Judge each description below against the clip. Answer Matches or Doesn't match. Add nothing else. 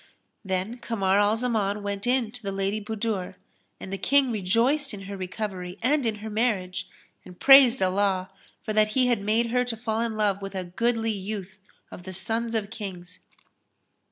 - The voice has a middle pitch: Doesn't match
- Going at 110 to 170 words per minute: Doesn't match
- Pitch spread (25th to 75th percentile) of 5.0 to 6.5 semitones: Doesn't match